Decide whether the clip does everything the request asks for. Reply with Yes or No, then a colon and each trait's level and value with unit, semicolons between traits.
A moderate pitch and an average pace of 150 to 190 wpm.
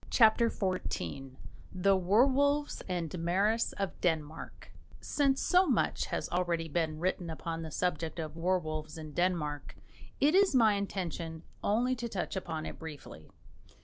No: medium, 180 Hz; average, 140 wpm